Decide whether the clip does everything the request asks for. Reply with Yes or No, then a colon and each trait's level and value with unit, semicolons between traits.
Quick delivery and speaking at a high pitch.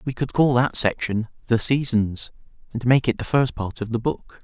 No: fast, 215 wpm; low, 120 Hz